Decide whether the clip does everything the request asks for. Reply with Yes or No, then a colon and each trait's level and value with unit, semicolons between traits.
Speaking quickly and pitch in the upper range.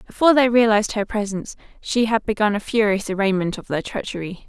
No: average, 190 wpm; high, 210 Hz